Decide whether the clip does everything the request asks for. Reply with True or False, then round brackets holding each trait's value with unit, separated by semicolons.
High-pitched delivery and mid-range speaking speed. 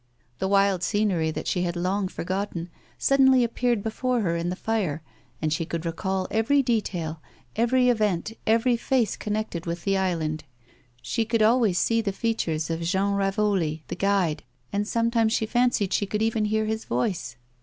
True (200 Hz; 170 wpm)